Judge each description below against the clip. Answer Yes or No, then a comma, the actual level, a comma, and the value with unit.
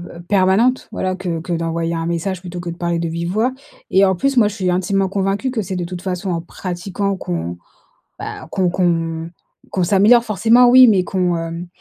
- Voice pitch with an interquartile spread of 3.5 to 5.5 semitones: No, average, 2.7 semitones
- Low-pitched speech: No, medium, 185 Hz